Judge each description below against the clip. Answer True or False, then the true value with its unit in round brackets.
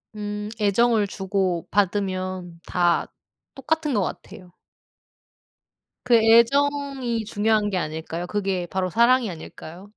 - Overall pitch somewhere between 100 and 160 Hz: False (205 Hz)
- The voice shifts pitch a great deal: False (4.1 semitones)